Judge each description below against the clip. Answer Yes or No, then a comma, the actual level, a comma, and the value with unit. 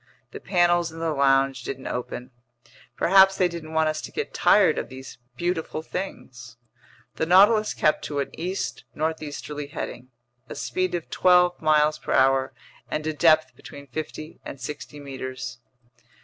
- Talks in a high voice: No, medium, 155 Hz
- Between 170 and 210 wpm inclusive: No, average, 155 wpm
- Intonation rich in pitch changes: No, average, 4.1 semitones